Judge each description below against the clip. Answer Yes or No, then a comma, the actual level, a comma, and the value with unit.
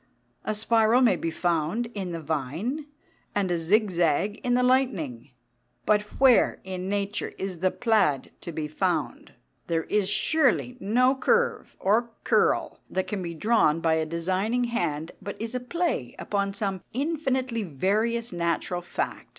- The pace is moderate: Yes, average, 155 wpm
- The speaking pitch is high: Yes, high, 200 Hz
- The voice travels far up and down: Yes, wide, 5.8 semitones